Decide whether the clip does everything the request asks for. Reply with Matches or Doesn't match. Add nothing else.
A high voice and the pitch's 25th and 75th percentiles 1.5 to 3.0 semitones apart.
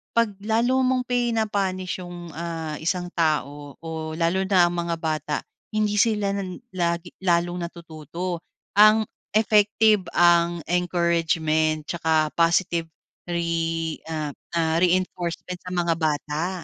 Doesn't match